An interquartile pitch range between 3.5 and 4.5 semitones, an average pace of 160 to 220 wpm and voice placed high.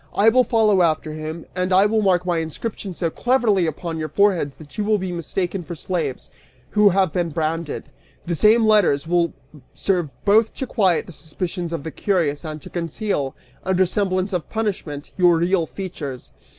No: average, 3.8 semitones; average, 180 wpm; medium, 180 Hz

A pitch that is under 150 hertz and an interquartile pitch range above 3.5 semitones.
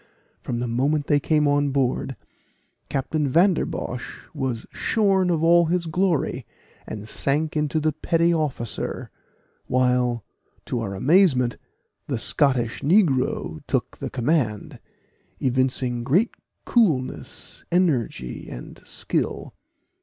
Yes: medium, 140 Hz; average, 4.8 semitones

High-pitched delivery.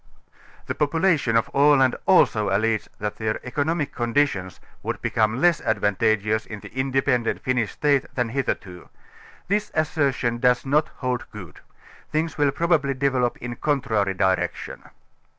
No: low, 125 Hz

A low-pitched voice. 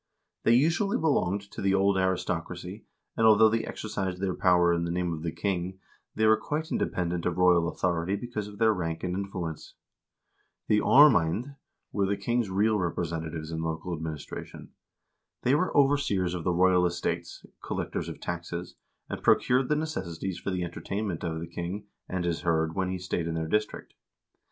Yes: very low, 90 Hz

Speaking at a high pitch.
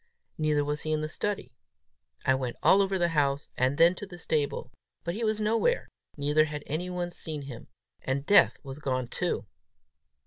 No: medium, 155 Hz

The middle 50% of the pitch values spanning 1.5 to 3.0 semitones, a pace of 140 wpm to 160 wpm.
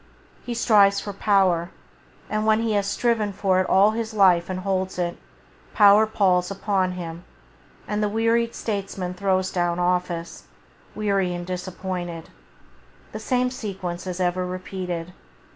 Yes: average, 2.7 semitones; average, 145 wpm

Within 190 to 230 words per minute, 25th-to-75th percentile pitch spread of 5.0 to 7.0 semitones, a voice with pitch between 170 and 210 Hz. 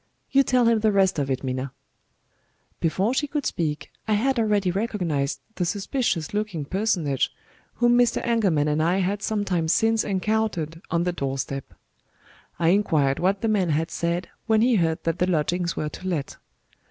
No: average, 180 wpm; average, 5.3 semitones; medium, 185 Hz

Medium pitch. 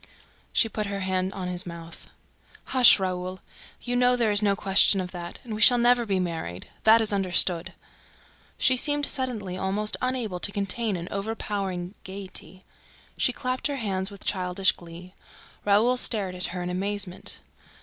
No: high, 195 Hz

